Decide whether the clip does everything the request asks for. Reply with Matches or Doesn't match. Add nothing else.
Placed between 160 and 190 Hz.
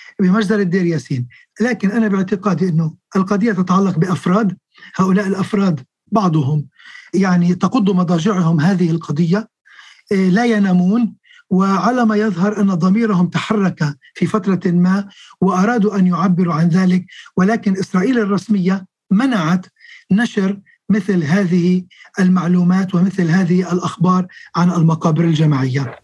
Matches